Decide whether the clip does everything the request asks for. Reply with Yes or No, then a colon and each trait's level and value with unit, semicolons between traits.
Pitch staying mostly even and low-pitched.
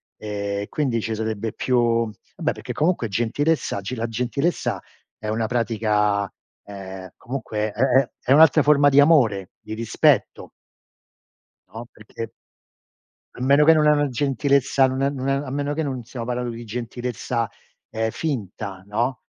No: average, 4.1 semitones; low, 120 Hz